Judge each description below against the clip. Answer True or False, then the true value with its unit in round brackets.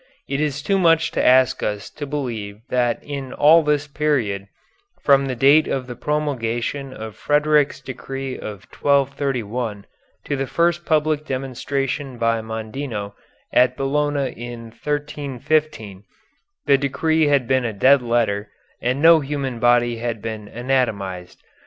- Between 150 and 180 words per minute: False (140 wpm)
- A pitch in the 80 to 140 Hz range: True (135 Hz)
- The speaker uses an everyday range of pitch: True (4.0 semitones)